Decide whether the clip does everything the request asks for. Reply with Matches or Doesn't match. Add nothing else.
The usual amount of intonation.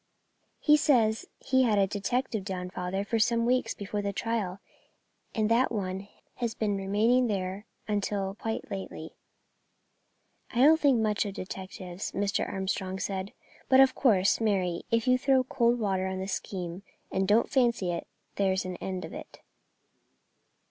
Matches